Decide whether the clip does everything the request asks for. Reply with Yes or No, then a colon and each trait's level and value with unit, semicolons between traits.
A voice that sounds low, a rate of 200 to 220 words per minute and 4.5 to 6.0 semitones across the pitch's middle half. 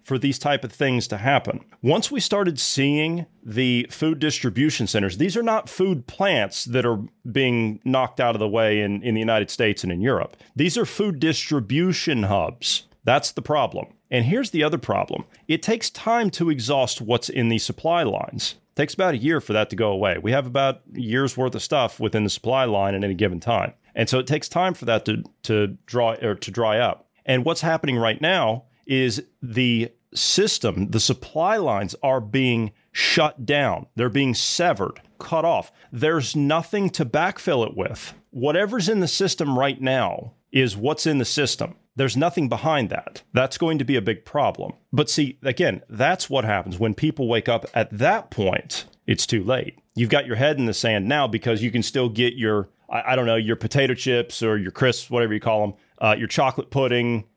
Yes: low, 130 Hz; fast, 205 wpm; average, 5.0 semitones